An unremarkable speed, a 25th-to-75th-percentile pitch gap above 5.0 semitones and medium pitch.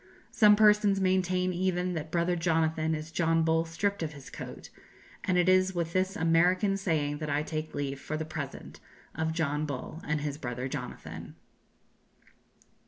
No: average, 165 wpm; average, 3.2 semitones; medium, 165 Hz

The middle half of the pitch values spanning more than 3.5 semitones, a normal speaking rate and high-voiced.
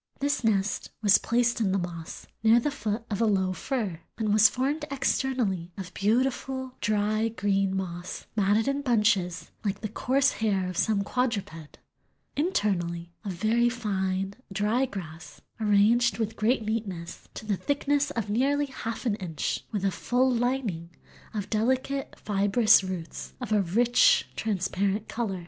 Yes: average, 4.1 semitones; average, 150 wpm; high, 215 Hz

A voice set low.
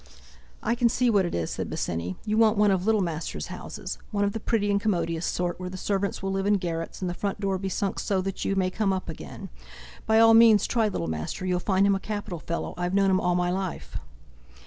No: high, 195 Hz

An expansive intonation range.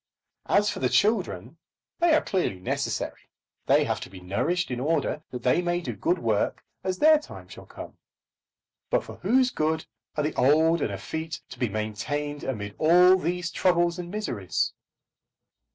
Yes: wide, 6.4 semitones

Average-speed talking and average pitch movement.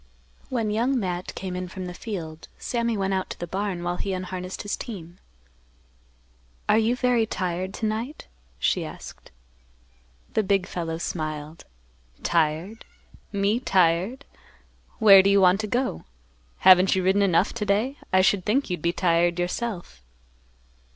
Yes: average, 150 wpm; average, 3.5 semitones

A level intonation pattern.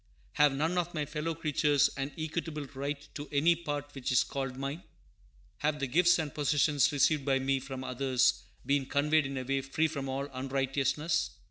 Yes: narrow, 2.1 semitones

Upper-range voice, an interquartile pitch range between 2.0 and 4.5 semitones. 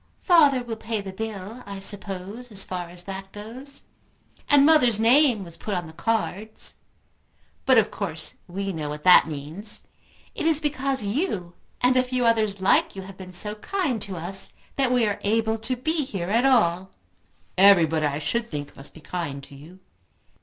No: high, 205 Hz; wide, 5.4 semitones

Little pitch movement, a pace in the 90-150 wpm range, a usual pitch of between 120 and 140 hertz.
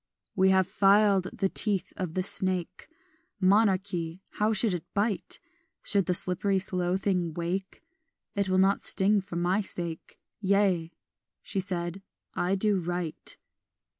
No: narrow, 2.0 semitones; slow, 135 wpm; high, 190 Hz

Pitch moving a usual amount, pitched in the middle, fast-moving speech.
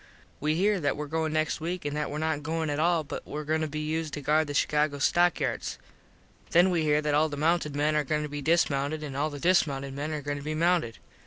No: narrow, 1.7 semitones; medium, 155 Hz; fast, 260 wpm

